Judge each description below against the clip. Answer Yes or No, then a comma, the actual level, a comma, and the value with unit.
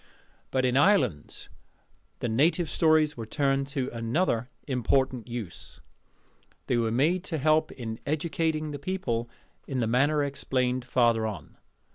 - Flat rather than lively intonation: No, average, 4.5 semitones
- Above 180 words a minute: No, slow, 135 wpm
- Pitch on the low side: Yes, low, 130 Hz